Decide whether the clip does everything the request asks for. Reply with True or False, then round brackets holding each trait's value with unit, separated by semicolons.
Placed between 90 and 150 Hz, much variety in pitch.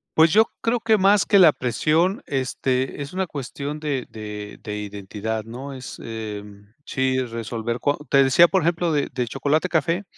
True (135 Hz; 6.7 semitones)